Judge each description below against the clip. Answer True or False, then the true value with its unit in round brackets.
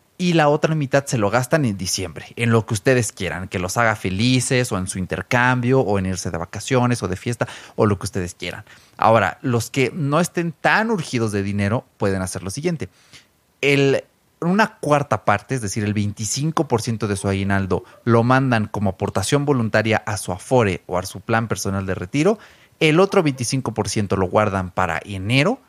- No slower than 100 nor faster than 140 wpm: False (190 wpm)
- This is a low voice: True (115 Hz)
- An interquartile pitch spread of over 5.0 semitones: True (5.4 semitones)